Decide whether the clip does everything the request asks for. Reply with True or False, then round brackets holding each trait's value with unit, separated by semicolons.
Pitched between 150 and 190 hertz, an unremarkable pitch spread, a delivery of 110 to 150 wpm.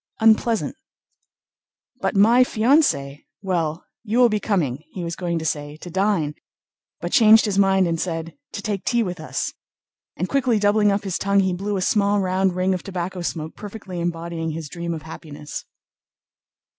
False (185 Hz; 3.9 semitones; 170 wpm)